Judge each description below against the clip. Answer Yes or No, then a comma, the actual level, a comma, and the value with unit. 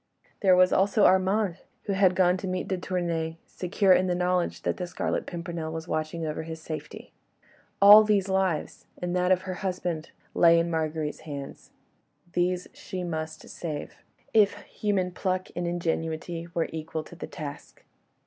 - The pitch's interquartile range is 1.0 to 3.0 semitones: Yes, narrow, 2.4 semitones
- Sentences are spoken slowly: No, average, 165 wpm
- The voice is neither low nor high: Yes, medium, 175 Hz